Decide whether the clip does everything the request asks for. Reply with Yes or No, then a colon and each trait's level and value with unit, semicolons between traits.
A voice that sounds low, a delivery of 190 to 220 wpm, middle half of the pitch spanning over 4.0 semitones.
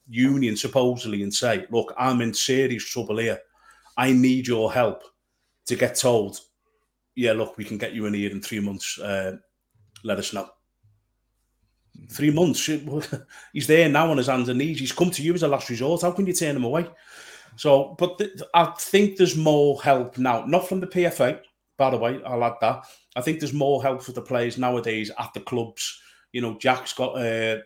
Yes: low, 130 Hz; average, 200 wpm; average, 4.7 semitones